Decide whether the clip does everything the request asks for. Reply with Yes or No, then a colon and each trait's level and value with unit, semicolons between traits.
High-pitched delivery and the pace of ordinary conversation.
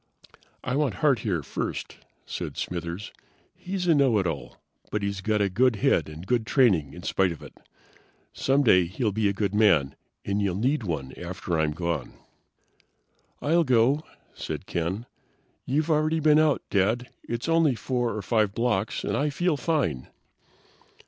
No: low, 110 Hz; average, 160 wpm